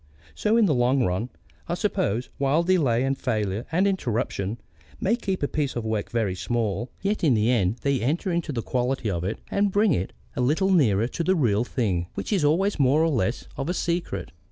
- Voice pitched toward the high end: No, low, 130 Hz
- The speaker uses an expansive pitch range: Yes, wide, 7.3 semitones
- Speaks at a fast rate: Yes, fast, 210 wpm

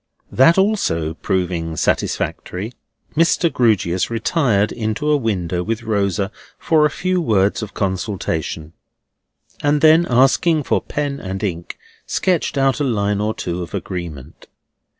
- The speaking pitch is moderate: No, low, 110 Hz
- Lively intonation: Yes, wide, 8.0 semitones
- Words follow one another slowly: Yes, slow, 130 wpm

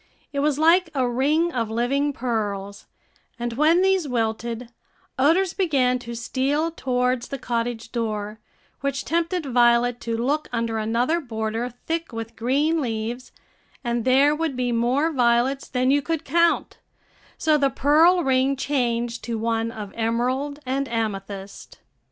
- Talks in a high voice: Yes, very high, 250 Hz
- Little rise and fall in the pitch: No, average, 3.9 semitones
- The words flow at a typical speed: Yes, average, 145 wpm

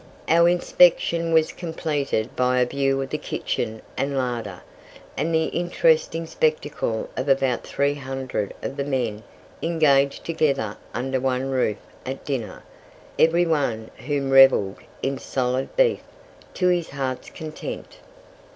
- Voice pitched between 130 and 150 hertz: Yes, low, 135 Hz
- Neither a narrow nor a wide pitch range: Yes, average, 3.9 semitones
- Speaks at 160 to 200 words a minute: No, slow, 135 wpm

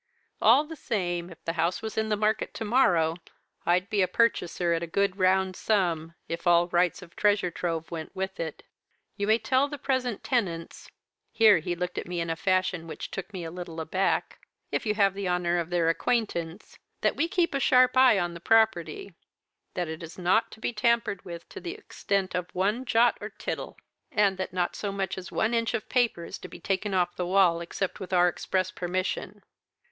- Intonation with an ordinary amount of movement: Yes, average, 4.0 semitones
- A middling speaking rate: No, fast, 210 wpm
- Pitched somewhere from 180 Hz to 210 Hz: Yes, medium, 185 Hz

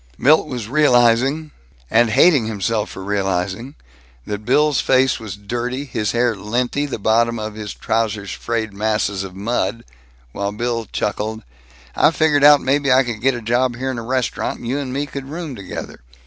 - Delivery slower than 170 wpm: No, average, 175 wpm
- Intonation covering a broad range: No, average, 3.8 semitones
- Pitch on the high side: No, low, 120 Hz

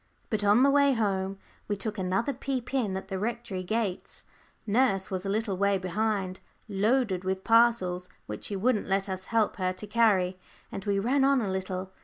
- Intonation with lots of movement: No, average, 3.5 semitones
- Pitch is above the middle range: Yes, high, 200 Hz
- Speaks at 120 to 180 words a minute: No, average, 190 wpm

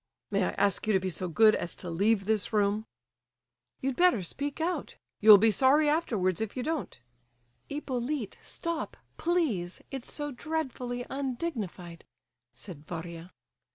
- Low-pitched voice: No, high, 225 Hz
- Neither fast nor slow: Yes, average, 145 wpm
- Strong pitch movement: Yes, wide, 7.3 semitones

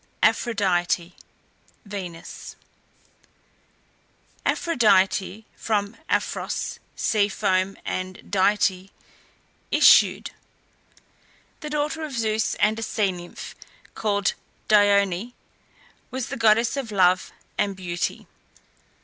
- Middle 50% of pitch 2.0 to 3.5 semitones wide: Yes, average, 3.2 semitones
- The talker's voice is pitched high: Yes, high, 205 Hz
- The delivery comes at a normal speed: No, slow, 85 wpm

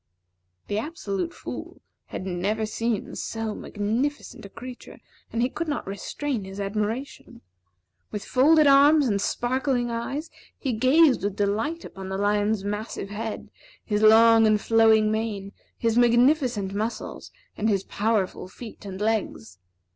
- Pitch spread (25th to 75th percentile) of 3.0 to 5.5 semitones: Yes, average, 3.6 semitones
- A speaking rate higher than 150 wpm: No, average, 140 wpm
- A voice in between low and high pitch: No, high, 220 Hz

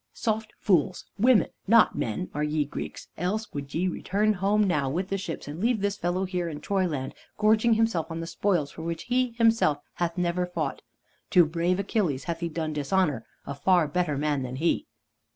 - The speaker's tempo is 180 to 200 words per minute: Yes, average, 190 wpm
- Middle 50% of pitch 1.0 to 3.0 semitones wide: No, average, 4.8 semitones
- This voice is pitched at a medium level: Yes, medium, 175 Hz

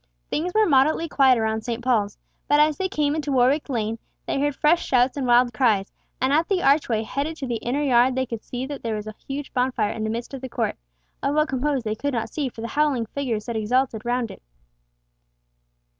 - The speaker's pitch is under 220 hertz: No, very high, 255 Hz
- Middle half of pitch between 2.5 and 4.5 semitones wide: Yes, average, 4.0 semitones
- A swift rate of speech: Yes, fast, 220 wpm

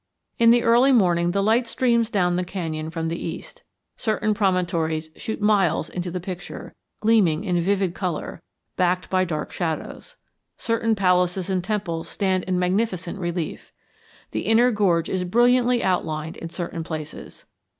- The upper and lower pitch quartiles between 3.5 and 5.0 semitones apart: Yes, average, 4.0 semitones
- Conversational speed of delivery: Yes, average, 150 wpm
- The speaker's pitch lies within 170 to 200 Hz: Yes, medium, 185 Hz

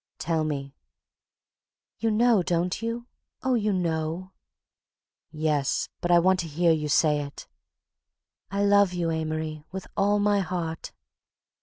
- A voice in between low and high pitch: Yes, medium, 175 Hz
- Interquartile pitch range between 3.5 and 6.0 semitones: Yes, average, 4.2 semitones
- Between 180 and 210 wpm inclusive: No, slow, 135 wpm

